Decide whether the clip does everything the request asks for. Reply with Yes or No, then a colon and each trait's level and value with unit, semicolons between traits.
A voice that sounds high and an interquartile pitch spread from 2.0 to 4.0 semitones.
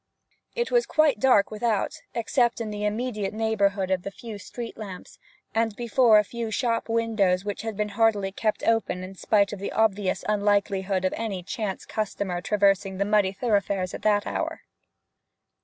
Yes: high, 210 Hz; narrow, 2.4 semitones